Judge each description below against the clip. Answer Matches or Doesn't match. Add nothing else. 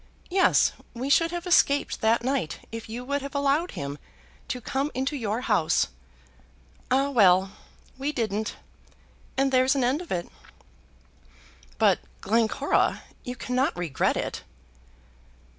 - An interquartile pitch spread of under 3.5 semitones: Doesn't match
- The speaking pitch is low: Doesn't match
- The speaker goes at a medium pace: Doesn't match